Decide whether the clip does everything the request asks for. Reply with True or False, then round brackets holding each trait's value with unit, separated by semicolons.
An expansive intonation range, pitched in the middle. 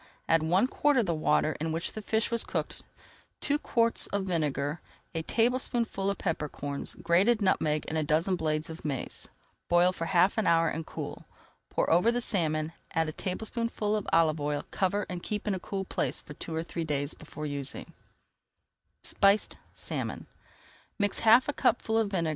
False (4.8 semitones; 170 Hz)